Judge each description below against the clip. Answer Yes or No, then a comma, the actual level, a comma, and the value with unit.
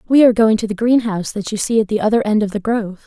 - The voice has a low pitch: No, high, 215 Hz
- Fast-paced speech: Yes, fast, 315 wpm